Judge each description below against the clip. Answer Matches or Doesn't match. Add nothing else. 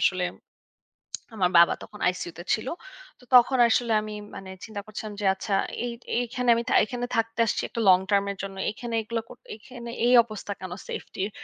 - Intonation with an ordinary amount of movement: Matches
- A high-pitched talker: Matches